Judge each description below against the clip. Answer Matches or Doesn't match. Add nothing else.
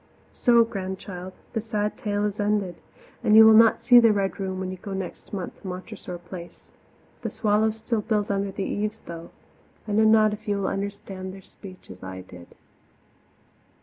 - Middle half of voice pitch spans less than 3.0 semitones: Matches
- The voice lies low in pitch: Doesn't match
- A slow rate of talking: Doesn't match